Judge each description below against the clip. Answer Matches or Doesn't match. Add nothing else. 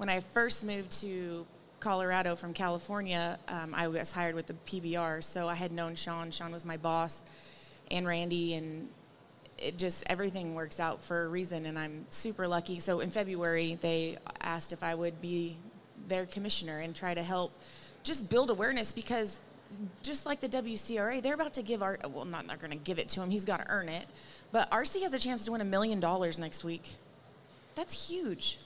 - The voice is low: Doesn't match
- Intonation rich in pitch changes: Doesn't match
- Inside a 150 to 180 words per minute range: Doesn't match